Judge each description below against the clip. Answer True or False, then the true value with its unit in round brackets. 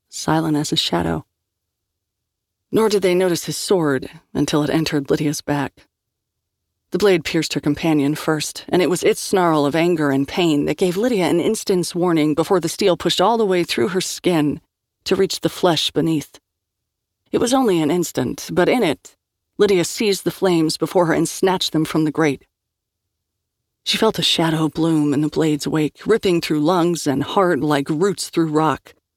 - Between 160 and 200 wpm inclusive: True (185 wpm)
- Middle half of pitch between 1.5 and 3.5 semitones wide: False (3.9 semitones)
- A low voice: False (155 Hz)